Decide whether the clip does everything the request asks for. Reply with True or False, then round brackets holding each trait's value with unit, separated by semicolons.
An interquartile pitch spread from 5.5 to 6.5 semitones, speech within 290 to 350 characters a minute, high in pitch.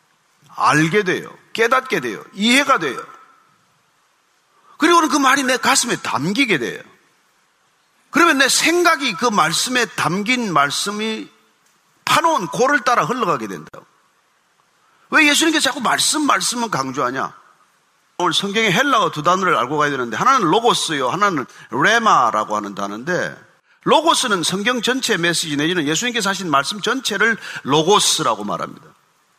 False (8.3 semitones; 305 characters per minute; 240 Hz)